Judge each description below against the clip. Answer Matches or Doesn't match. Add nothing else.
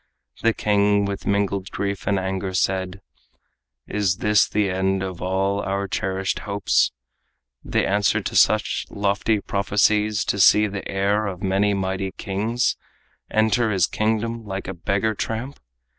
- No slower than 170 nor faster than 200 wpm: Doesn't match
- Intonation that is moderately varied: Doesn't match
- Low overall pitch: Matches